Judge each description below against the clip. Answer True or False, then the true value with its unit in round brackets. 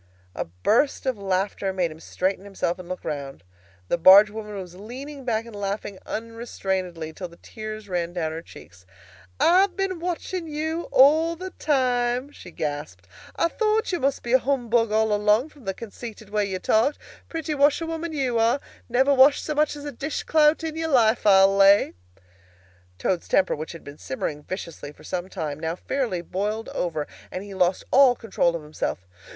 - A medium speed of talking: True (180 wpm)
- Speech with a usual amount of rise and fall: False (7.4 semitones)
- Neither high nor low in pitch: False (215 Hz)